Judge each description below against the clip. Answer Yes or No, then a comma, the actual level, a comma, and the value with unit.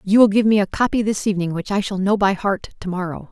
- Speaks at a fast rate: Yes, fast, 270 wpm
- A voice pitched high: Yes, high, 200 Hz